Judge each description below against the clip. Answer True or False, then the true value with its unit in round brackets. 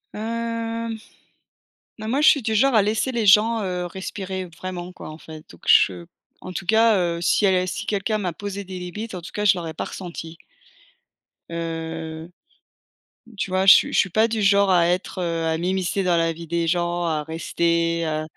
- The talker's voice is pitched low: False (185 Hz)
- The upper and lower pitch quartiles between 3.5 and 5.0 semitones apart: True (3.8 semitones)